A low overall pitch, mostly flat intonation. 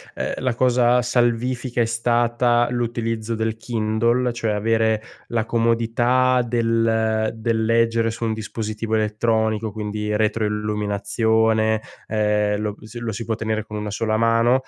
Yes: low, 115 Hz; narrow, 1.5 semitones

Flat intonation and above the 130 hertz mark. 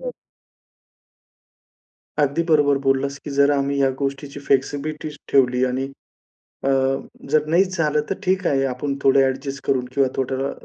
Yes: narrow, 1.8 semitones; medium, 140 Hz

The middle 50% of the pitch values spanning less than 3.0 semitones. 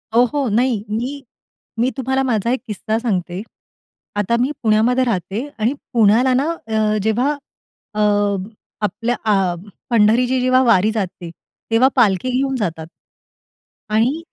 No: average, 3.4 semitones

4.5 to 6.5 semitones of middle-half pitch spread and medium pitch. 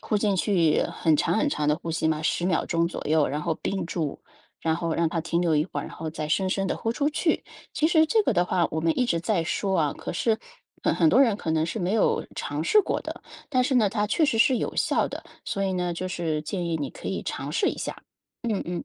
Yes: average, 5.1 semitones; medium, 175 Hz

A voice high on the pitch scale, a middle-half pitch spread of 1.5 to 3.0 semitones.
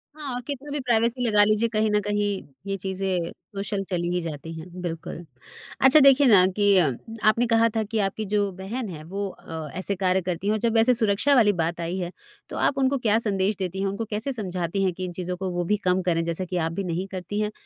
No: high, 195 Hz; average, 3.7 semitones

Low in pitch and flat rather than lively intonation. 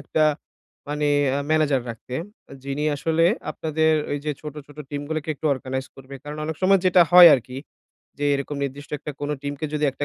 No: medium, 145 Hz; narrow, 2.2 semitones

